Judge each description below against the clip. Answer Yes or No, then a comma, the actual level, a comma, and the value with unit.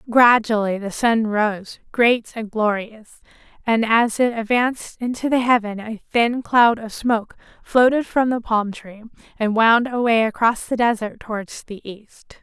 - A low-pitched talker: No, high, 225 Hz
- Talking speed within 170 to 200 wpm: No, average, 160 wpm